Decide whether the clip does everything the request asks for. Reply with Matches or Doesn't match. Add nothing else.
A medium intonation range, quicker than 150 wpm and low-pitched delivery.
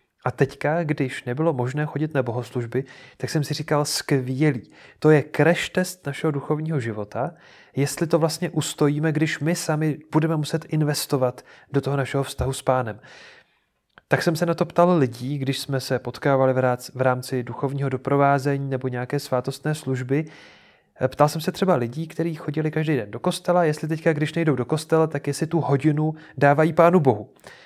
Doesn't match